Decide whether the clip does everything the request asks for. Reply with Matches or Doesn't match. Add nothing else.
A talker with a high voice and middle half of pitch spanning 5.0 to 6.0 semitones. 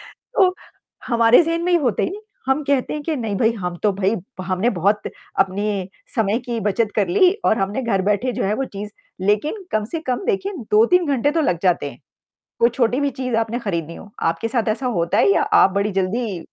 Matches